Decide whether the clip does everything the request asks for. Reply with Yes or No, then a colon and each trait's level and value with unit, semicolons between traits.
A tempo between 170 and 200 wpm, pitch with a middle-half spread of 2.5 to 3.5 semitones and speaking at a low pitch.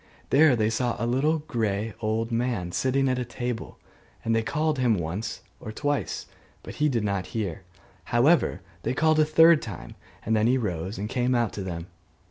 No: average, 195 wpm; average, 4.0 semitones; low, 115 Hz